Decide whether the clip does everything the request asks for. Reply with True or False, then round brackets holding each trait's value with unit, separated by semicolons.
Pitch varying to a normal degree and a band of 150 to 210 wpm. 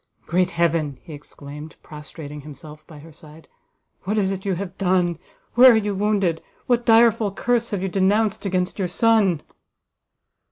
True (4.7 semitones; 160 wpm)